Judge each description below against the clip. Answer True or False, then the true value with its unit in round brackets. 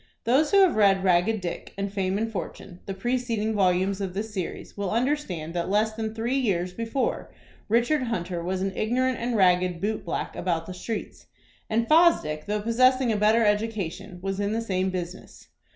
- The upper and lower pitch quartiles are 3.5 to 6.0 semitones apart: True (3.8 semitones)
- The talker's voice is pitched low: False (210 Hz)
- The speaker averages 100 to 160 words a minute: False (185 wpm)